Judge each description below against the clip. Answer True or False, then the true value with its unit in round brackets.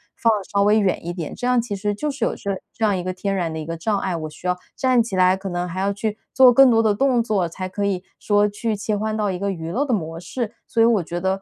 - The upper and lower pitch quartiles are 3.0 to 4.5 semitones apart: True (3.6 semitones)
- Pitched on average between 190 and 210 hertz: True (200 Hz)